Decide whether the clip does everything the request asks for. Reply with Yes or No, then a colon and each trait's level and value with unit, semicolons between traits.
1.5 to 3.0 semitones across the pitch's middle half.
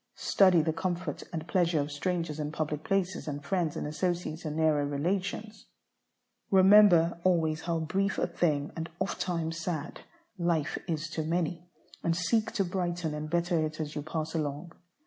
Yes: narrow, 2.5 semitones